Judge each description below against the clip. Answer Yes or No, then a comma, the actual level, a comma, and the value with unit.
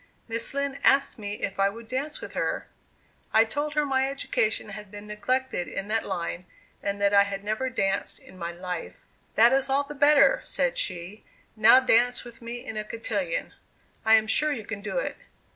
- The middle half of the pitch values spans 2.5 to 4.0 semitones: No, average, 4.8 semitones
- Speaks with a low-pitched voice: No, high, 225 Hz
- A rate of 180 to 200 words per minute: Yes, average, 195 wpm